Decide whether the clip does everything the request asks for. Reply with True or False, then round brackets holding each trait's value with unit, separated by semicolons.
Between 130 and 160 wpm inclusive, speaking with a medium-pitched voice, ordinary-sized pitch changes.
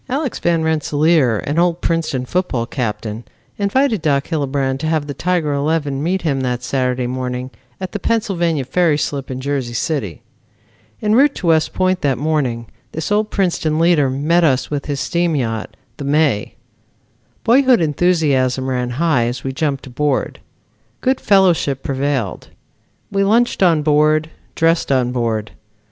True (155 wpm; 150 Hz; 4.7 semitones)